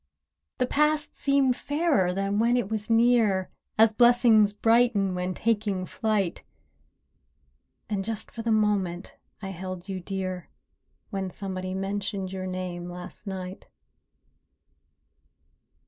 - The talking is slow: Yes, slow, 115 wpm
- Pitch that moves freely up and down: No, average, 3.4 semitones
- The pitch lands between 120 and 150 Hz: No, high, 200 Hz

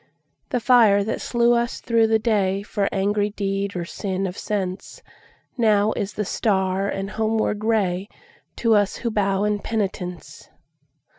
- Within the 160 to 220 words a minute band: No, slow, 135 wpm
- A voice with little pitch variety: Yes, narrow, 2.3 semitones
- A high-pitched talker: Yes, high, 205 Hz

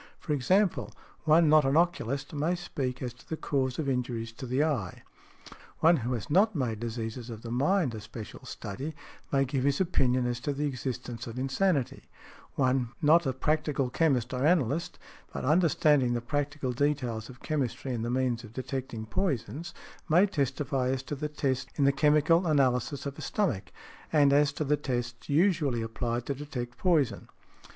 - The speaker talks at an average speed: Yes, average, 175 wpm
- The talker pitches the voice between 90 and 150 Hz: Yes, low, 135 Hz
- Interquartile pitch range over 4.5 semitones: No, average, 3.7 semitones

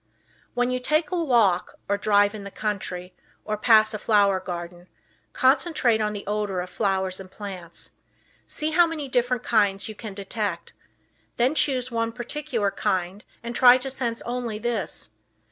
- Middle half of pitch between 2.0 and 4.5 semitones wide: Yes, average, 4.0 semitones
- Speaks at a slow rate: No, average, 160 wpm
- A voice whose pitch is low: No, high, 215 Hz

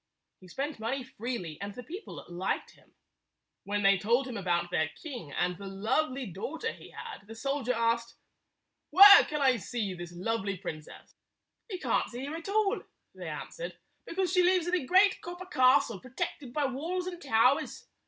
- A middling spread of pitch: No, wide, 8.5 semitones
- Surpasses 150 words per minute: Yes, average, 185 wpm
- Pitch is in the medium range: No, very high, 255 Hz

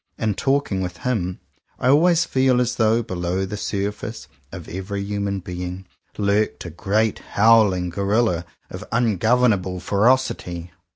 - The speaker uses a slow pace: Yes, slow, 130 wpm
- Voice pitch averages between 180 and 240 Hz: No, low, 100 Hz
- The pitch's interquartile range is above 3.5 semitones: Yes, average, 3.9 semitones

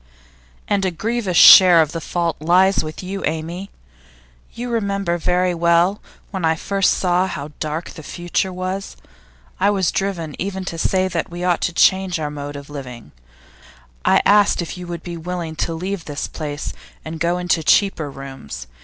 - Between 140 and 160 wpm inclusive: No, average, 180 wpm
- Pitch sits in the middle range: Yes, medium, 175 Hz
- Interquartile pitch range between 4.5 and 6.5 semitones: No, average, 3.0 semitones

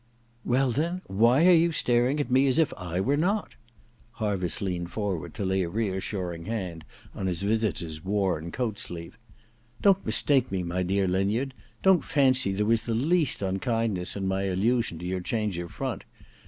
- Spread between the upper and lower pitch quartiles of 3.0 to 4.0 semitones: No, average, 5.3 semitones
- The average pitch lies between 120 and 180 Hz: No, low, 105 Hz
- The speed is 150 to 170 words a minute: No, average, 185 wpm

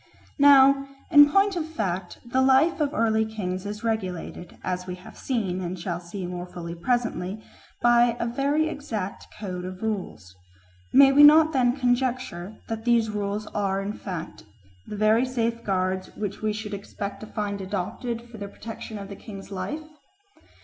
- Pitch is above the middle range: Yes, high, 215 Hz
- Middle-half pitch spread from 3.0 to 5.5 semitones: Yes, average, 4.8 semitones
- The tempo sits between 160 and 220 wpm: Yes, average, 170 wpm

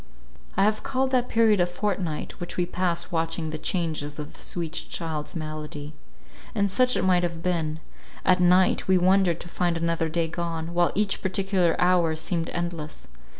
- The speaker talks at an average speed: Yes, average, 165 wpm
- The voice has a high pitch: No, medium, 175 Hz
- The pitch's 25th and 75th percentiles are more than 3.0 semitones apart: No, narrow, 2.4 semitones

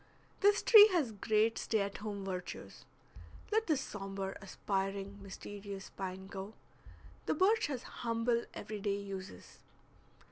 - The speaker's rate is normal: No, slow, 130 wpm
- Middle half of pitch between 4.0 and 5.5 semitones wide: No, average, 3.3 semitones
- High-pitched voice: Yes, high, 205 Hz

